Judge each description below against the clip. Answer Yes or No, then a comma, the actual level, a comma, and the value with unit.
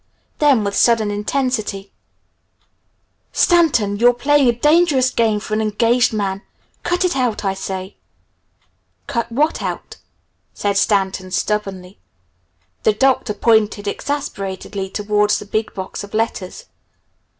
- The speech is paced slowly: Yes, slow, 120 wpm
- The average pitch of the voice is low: No, high, 215 Hz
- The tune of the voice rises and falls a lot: No, average, 3.9 semitones